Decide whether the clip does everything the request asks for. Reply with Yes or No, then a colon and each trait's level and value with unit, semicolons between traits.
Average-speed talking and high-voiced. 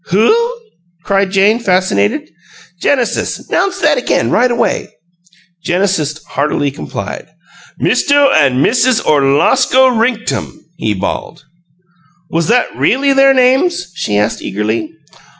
No: slow, 110 wpm; high, 200 Hz